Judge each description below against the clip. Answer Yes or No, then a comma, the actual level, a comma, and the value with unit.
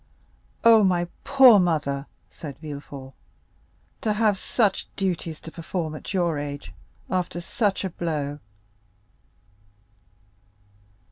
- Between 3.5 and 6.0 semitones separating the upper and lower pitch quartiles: Yes, average, 4.7 semitones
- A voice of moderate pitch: Yes, medium, 175 Hz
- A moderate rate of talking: No, slow, 105 wpm